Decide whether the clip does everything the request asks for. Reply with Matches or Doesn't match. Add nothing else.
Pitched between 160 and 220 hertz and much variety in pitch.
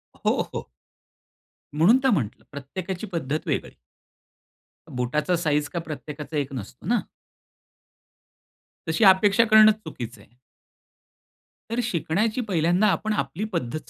Matches